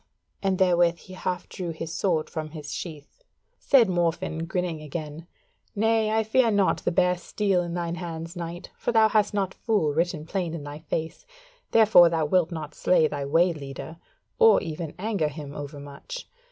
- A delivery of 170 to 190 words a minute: Yes, average, 180 wpm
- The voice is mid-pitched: Yes, medium, 170 Hz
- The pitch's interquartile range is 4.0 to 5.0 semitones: No, average, 3.4 semitones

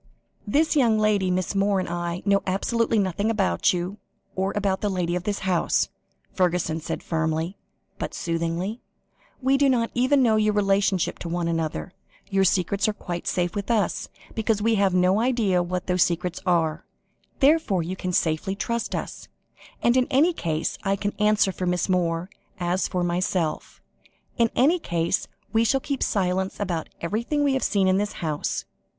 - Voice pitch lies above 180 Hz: Yes, high, 190 Hz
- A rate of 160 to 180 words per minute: Yes, average, 175 wpm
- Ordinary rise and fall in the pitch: Yes, average, 3.7 semitones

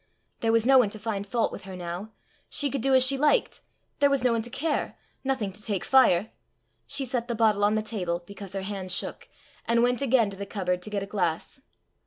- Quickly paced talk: Yes, fast, 235 wpm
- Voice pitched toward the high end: Yes, high, 220 Hz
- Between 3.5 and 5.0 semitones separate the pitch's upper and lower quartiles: Yes, average, 4.5 semitones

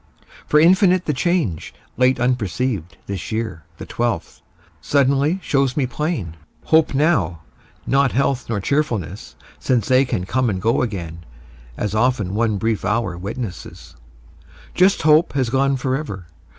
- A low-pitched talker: Yes, low, 125 Hz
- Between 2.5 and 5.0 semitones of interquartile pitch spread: No, wide, 5.6 semitones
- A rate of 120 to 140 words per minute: Yes, slow, 135 wpm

